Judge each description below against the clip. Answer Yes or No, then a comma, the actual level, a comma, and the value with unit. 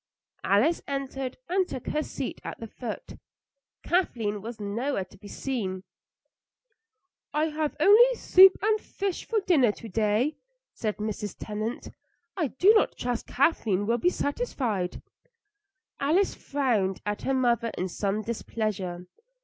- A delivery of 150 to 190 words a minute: No, slow, 135 wpm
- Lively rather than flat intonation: Yes, wide, 6.7 semitones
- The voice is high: Yes, high, 240 Hz